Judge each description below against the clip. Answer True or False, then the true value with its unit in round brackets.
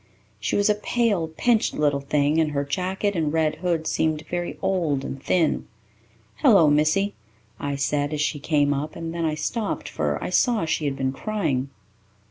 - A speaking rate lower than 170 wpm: False (180 wpm)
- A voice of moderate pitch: True (160 Hz)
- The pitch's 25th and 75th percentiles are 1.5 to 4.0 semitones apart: False (4.5 semitones)